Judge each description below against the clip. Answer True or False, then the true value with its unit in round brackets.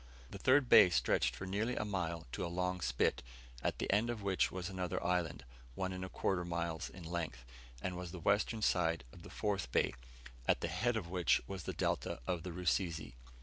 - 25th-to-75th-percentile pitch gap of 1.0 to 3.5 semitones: True (2.5 semitones)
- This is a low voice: True (90 Hz)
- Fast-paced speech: True (210 wpm)